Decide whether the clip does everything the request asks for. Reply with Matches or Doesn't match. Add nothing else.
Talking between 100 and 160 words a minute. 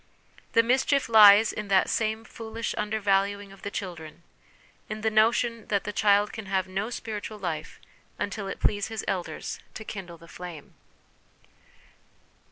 Matches